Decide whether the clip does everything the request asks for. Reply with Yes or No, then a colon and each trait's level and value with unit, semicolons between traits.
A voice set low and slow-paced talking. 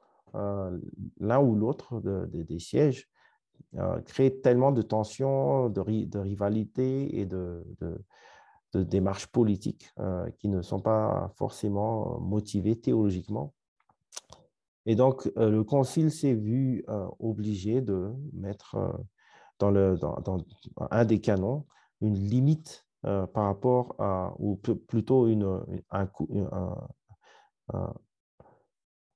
Yes: low, 105 Hz; slow, 135 wpm